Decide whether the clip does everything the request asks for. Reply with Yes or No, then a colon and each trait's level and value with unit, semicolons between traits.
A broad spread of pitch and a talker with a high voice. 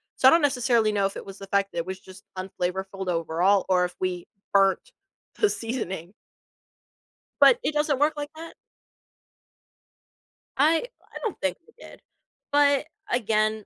Yes: wide, 7.2 semitones; high, 205 Hz